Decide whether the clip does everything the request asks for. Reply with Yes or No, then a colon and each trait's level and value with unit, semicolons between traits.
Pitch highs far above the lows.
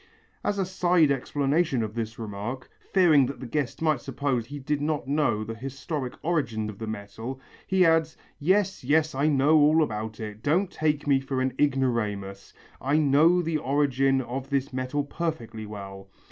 No: average, 4.9 semitones